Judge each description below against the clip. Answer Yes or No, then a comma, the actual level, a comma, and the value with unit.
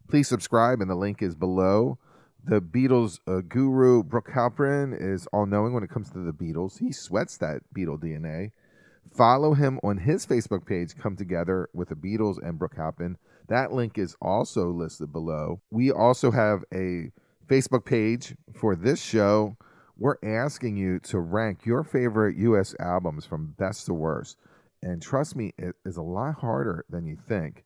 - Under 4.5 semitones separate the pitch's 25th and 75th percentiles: No, average, 5.3 semitones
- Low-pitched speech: Yes, low, 105 Hz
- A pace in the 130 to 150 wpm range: No, average, 175 wpm